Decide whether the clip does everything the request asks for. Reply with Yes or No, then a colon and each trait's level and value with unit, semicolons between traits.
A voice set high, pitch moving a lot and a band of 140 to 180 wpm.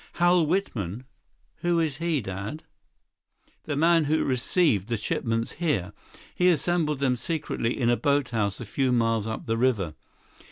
No: low, 130 Hz; wide, 6.1 semitones; average, 150 wpm